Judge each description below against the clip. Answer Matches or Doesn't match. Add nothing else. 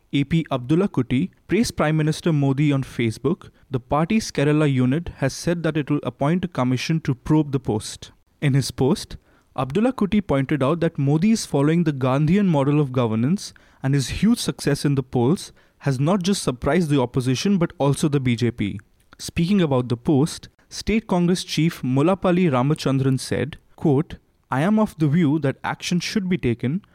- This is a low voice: Doesn't match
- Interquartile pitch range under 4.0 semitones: Doesn't match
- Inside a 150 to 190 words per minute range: Matches